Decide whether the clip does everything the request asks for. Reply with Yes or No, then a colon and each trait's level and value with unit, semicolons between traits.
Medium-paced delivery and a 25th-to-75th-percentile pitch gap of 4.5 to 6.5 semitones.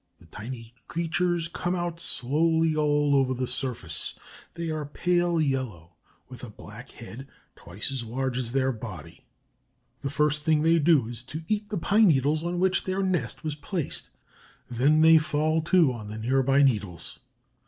Yes: average, 170 wpm; average, 5.0 semitones